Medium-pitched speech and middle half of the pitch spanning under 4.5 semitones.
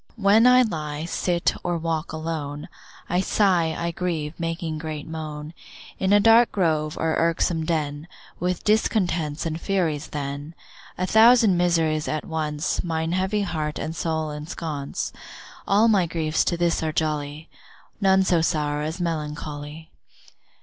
Yes: medium, 160 Hz; average, 2.8 semitones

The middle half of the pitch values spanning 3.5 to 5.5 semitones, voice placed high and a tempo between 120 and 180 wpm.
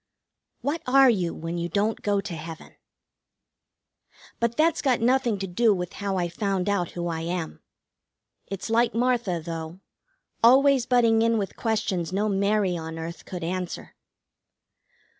Yes: average, 5.1 semitones; high, 200 Hz; average, 150 wpm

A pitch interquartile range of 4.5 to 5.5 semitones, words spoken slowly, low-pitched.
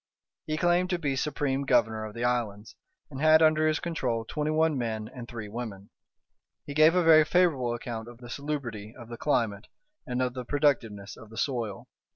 No: average, 5.1 semitones; average, 190 wpm; low, 125 Hz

